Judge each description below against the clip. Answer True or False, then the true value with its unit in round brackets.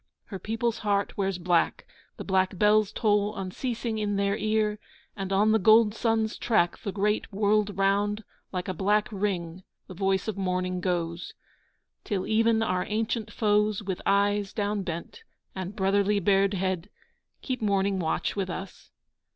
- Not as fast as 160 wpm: True (150 wpm)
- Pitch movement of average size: False (2.0 semitones)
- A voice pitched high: True (200 Hz)